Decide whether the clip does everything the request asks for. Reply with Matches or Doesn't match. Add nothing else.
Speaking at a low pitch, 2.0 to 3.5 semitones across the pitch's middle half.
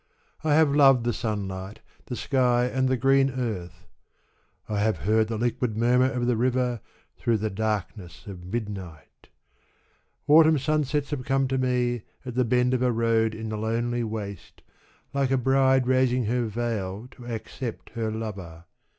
Matches